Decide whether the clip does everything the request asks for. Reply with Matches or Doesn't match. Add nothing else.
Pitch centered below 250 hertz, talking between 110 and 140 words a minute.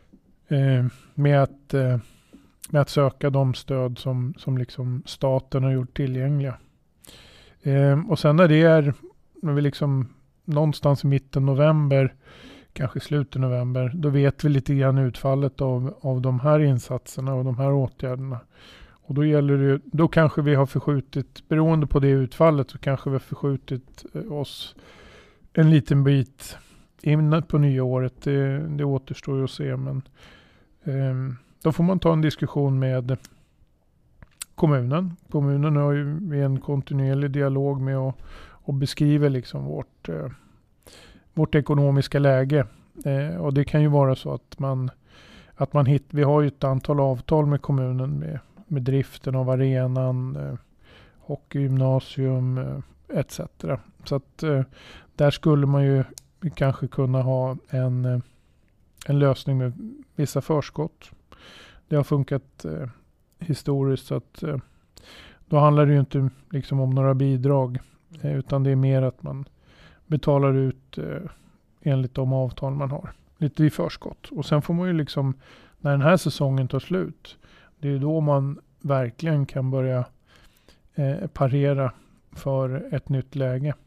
Doesn't match